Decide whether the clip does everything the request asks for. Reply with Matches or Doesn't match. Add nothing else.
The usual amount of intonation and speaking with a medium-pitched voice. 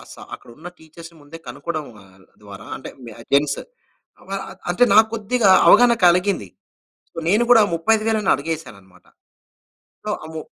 Doesn't match